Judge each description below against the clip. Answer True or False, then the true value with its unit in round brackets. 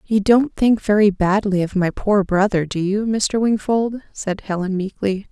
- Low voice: False (205 Hz)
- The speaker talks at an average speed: True (180 wpm)